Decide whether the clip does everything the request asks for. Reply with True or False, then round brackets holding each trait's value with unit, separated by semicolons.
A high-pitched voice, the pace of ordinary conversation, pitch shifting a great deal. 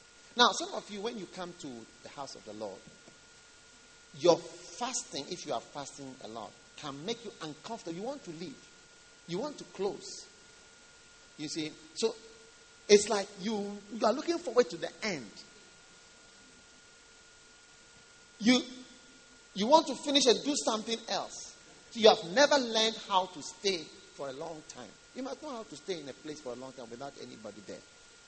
True (210 Hz; 175 wpm; 7.0 semitones)